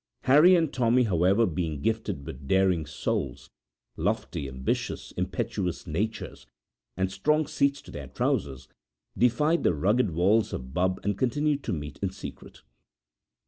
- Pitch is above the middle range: No, very low, 95 Hz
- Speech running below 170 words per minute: Yes, average, 140 wpm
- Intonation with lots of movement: Yes, wide, 7.3 semitones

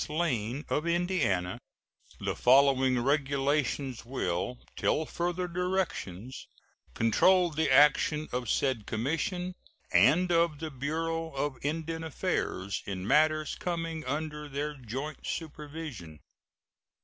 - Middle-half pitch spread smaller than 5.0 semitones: Yes, average, 4.2 semitones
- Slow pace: Yes, slow, 110 wpm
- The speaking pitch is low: No, medium, 150 Hz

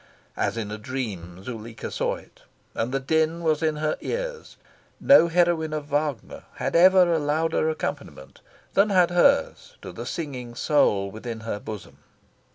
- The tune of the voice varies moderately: No, wide, 6.9 semitones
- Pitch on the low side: No, medium, 150 Hz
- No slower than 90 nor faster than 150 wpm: No, average, 160 wpm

